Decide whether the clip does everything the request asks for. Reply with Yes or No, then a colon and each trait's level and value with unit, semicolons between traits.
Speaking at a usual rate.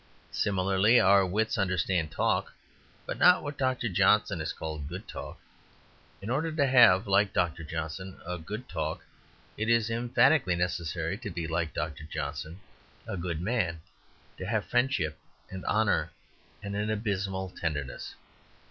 Yes: average, 145 wpm